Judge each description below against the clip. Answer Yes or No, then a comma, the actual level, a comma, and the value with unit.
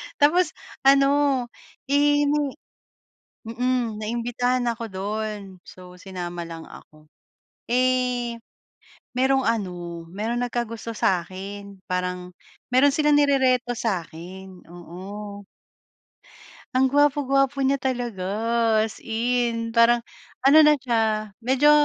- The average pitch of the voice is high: Yes, high, 235 Hz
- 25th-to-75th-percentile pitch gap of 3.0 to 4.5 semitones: No, average, 5.3 semitones